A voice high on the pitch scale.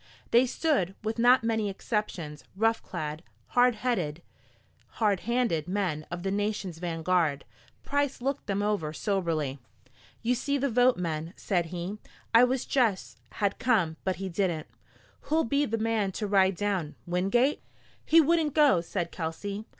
Yes: high, 200 Hz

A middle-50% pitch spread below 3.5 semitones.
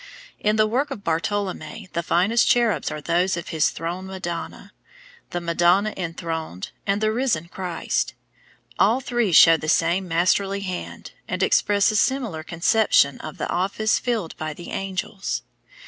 No: average, 4.2 semitones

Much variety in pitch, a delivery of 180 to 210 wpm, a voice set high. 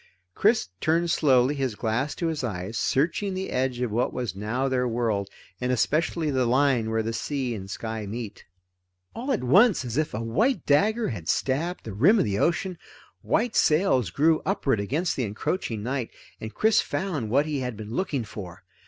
No: wide, 6.4 semitones; average, 190 wpm; low, 130 Hz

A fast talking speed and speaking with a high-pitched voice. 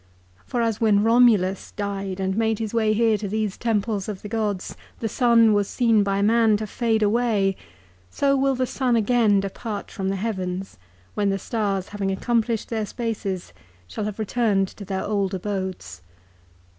No: average, 170 wpm; high, 210 Hz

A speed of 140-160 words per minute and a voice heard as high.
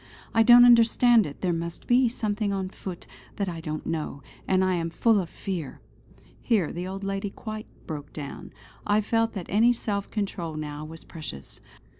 No: average, 180 wpm; high, 195 Hz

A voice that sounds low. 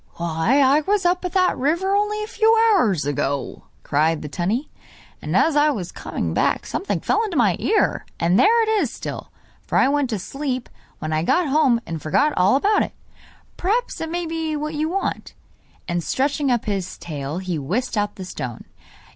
No: very high, 270 Hz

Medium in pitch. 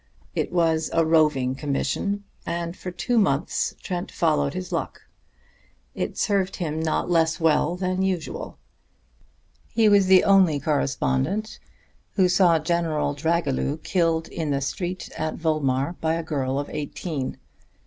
Yes: medium, 165 Hz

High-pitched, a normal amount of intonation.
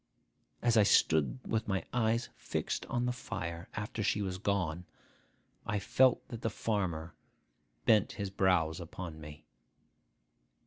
No: very low, 95 Hz; average, 4.7 semitones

